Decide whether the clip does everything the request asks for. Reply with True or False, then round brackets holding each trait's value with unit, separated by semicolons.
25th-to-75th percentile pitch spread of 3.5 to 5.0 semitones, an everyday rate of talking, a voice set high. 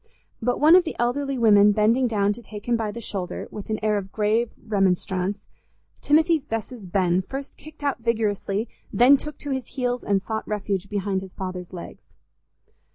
True (3.9 semitones; 180 wpm; 215 Hz)